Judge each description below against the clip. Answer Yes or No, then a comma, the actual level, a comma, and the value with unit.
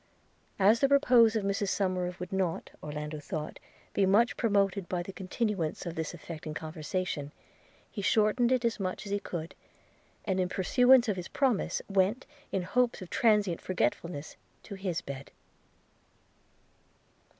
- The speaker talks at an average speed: Yes, average, 150 wpm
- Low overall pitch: No, high, 190 Hz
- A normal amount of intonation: Yes, average, 4.0 semitones